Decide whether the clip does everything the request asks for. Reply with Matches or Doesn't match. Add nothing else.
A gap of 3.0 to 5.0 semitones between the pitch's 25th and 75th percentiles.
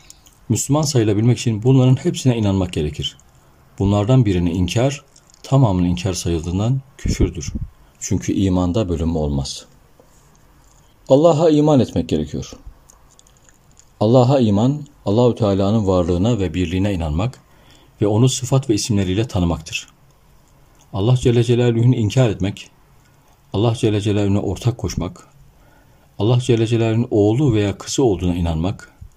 Doesn't match